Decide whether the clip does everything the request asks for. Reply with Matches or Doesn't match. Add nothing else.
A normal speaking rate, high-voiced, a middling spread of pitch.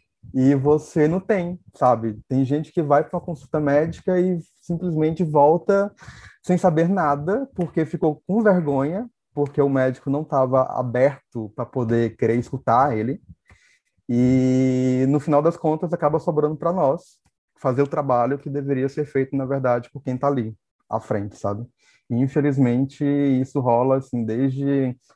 Doesn't match